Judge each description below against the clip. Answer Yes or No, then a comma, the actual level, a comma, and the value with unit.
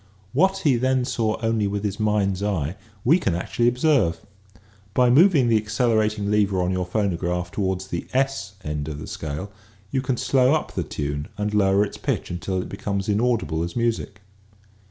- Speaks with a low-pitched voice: Yes, low, 105 Hz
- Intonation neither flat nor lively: Yes, average, 4.7 semitones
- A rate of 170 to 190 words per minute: Yes, average, 175 wpm